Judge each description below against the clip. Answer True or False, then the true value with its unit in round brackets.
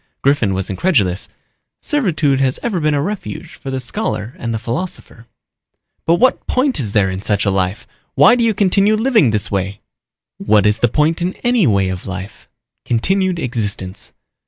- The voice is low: True (130 Hz)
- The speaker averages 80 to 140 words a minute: False (175 wpm)